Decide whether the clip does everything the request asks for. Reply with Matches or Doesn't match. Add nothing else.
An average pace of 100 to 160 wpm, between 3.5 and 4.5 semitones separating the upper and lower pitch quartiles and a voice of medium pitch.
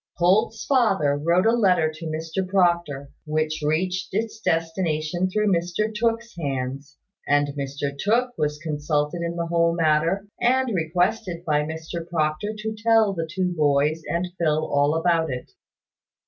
Matches